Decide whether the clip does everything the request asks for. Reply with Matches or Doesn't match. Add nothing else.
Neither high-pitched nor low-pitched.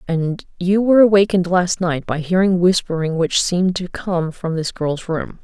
Matches